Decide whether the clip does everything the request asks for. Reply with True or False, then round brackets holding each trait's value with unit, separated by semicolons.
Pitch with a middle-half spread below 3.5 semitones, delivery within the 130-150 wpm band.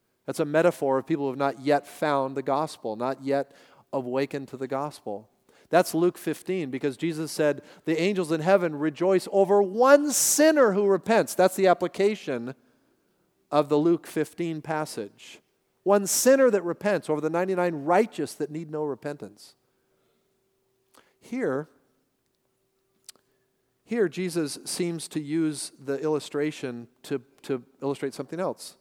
False (4.3 semitones; 140 wpm)